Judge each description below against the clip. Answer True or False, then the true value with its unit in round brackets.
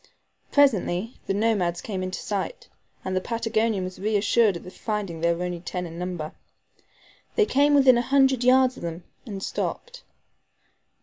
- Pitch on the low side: False (205 Hz)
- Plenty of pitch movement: True (5.7 semitones)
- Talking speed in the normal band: True (160 wpm)